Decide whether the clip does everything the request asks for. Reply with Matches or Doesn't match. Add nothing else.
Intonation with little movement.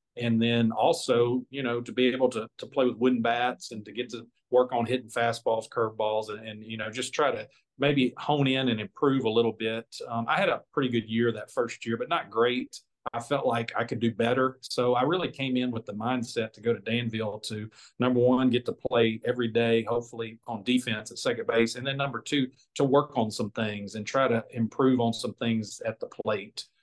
Matches